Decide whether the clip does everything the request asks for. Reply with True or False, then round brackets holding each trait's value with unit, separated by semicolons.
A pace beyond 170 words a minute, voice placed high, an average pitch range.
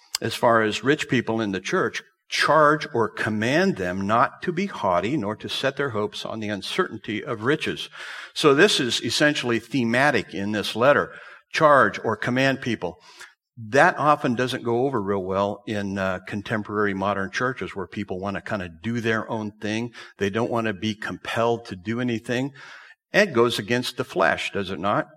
False (185 wpm; 110 Hz; 3.3 semitones)